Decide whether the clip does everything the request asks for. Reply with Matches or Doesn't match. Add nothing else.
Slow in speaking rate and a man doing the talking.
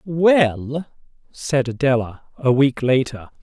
Matches